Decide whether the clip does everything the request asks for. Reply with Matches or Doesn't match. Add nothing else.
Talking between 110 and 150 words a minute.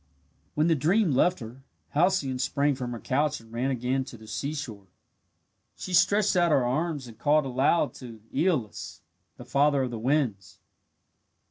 Doesn't match